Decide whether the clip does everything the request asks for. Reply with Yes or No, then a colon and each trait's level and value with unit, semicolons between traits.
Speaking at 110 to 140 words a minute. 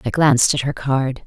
No: fast, 240 wpm